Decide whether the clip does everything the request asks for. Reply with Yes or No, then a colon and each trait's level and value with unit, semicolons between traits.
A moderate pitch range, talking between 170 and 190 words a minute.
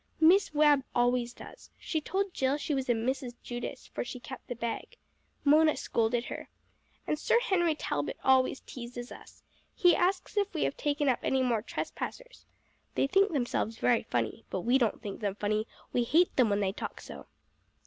Yes: average, 4.9 semitones; average, 185 wpm